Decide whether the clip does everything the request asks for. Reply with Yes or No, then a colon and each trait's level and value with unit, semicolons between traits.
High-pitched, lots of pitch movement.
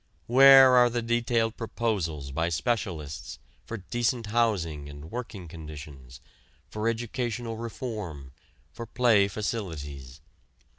No: low, 105 Hz; wide, 7.4 semitones